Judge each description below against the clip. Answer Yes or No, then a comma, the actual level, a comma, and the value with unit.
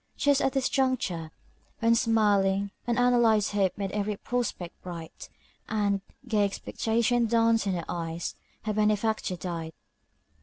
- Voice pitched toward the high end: Yes, high, 210 Hz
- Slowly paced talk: Yes, slow, 125 wpm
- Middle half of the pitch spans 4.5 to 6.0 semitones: No, average, 3.2 semitones